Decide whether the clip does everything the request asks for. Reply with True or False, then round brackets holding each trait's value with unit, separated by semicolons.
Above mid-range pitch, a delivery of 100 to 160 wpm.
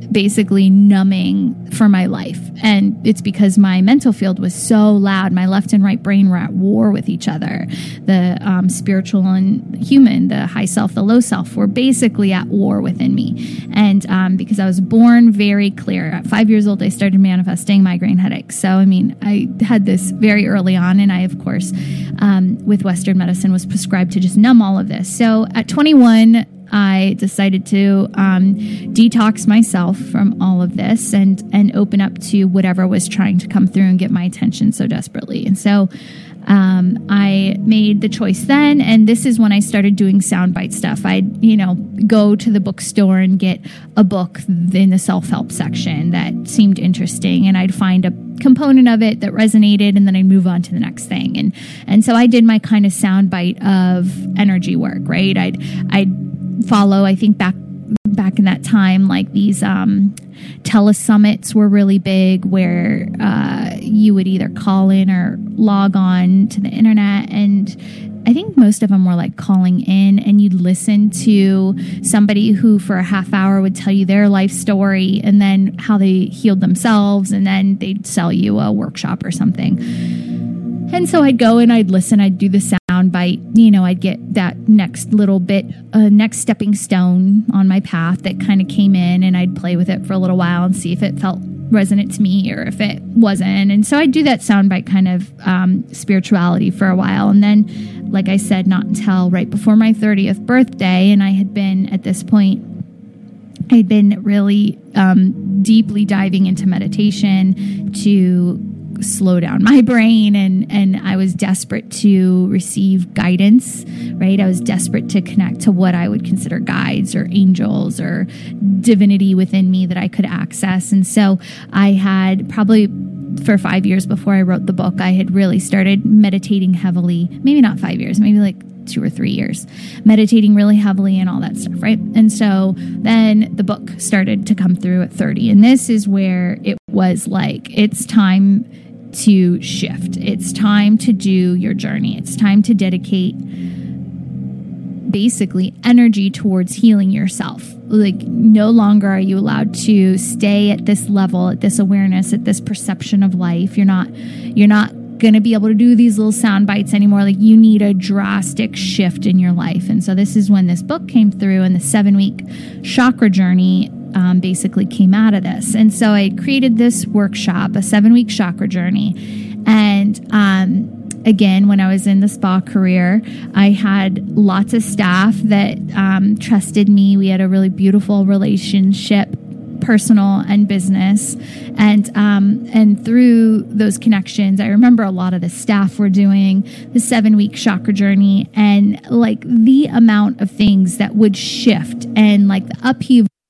False (200 Hz; 185 wpm)